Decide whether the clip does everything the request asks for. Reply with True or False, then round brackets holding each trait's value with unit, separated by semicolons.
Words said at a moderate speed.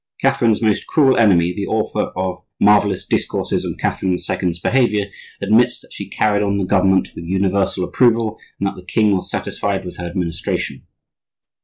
True (170 wpm)